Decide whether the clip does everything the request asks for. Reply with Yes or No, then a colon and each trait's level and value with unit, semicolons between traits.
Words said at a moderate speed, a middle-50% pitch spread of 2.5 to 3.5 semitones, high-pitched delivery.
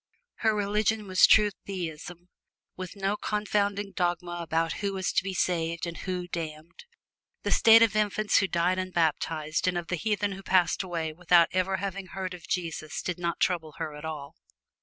No: average, 180 wpm; average, 2.8 semitones; medium, 180 Hz